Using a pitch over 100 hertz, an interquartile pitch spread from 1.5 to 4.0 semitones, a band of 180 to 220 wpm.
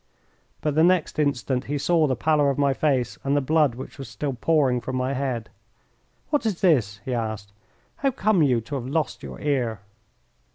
Yes: medium, 140 Hz; average, 3.6 semitones; average, 195 wpm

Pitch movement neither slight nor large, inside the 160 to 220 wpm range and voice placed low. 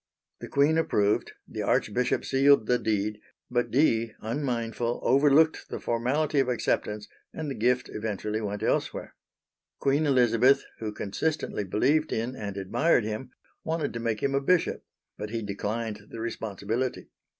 No: average, 4.4 semitones; average, 145 wpm; low, 120 Hz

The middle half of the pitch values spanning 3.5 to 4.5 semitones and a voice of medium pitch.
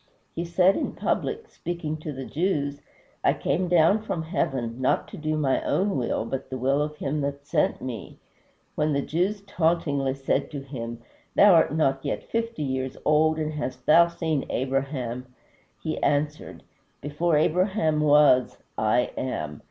Yes: average, 3.8 semitones; medium, 150 Hz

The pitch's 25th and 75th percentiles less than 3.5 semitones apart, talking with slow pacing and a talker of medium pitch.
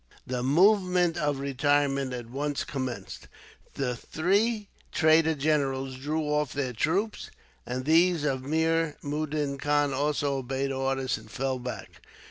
Yes: average, 2.9 semitones; slow, 130 wpm; medium, 145 Hz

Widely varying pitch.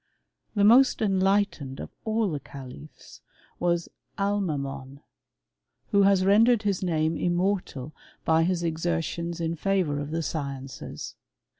No: average, 4.6 semitones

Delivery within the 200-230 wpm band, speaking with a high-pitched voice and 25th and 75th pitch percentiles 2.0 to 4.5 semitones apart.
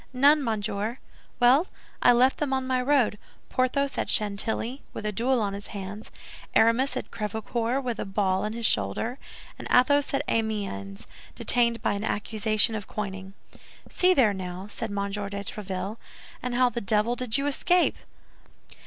No: average, 160 wpm; high, 225 Hz; average, 3.9 semitones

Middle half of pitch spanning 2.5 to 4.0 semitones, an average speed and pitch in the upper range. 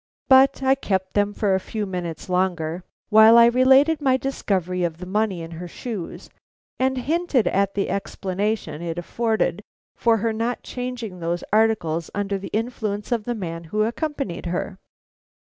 No: average, 4.8 semitones; average, 160 wpm; high, 205 Hz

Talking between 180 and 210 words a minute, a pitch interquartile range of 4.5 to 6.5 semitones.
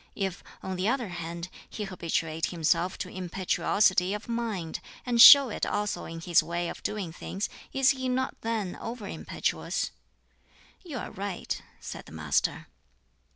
No: average, 155 wpm; average, 5.0 semitones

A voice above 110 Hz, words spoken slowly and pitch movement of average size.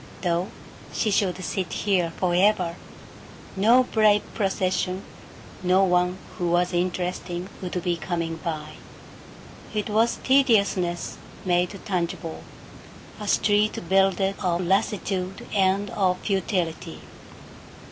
No: medium, 185 Hz; slow, 105 wpm; narrow, 2.3 semitones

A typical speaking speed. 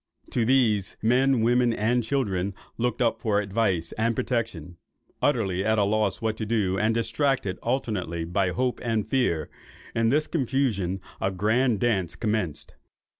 Yes: average, 150 wpm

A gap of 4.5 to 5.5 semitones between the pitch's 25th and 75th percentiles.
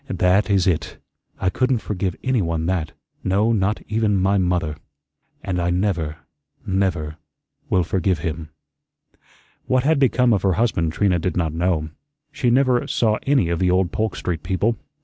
No: average, 4.0 semitones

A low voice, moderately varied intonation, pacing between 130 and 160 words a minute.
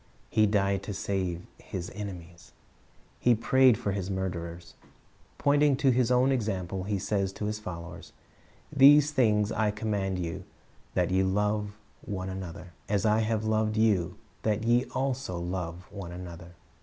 Yes: low, 100 Hz; average, 3.4 semitones; average, 150 wpm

